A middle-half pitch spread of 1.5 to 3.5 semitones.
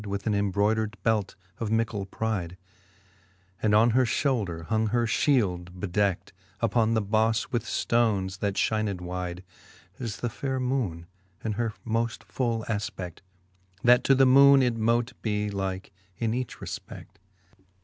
Yes: average, 3.1 semitones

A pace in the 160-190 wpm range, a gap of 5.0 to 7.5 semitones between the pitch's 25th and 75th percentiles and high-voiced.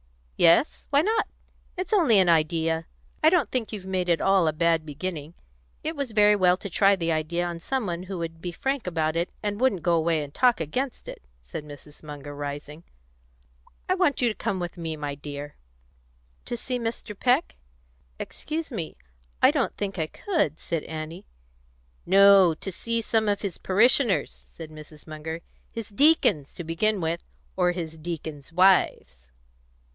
No: average, 175 wpm; wide, 5.5 semitones; medium, 175 Hz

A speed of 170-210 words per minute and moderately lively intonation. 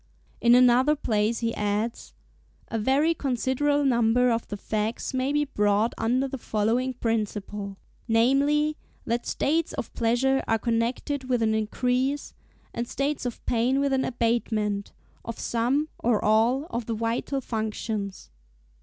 No: average, 140 wpm; average, 3.2 semitones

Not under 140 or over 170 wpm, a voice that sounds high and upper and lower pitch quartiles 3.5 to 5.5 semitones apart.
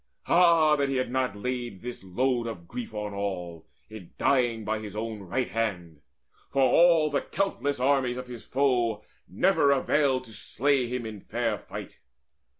No: average, 165 wpm; low, 120 Hz; average, 4.4 semitones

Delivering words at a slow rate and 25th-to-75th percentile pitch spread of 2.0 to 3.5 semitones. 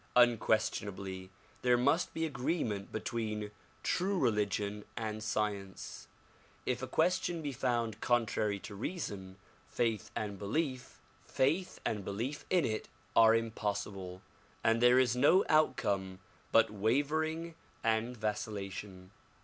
No: slow, 110 wpm; average, 3.9 semitones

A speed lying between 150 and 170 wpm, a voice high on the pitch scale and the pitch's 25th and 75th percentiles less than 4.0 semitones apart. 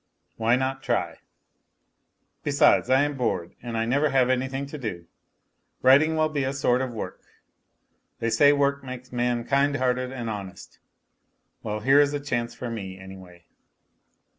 No: average, 160 wpm; low, 130 Hz; average, 3.3 semitones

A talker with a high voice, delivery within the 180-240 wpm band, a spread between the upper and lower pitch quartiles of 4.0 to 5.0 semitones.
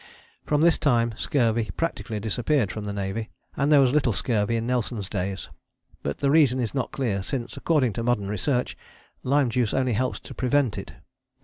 No: low, 120 Hz; average, 185 wpm; average, 4.3 semitones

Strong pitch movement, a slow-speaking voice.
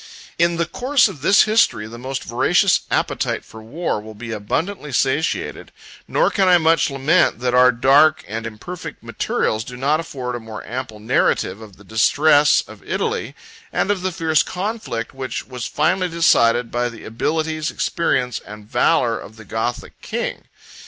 No: wide, 6.4 semitones; average, 165 wpm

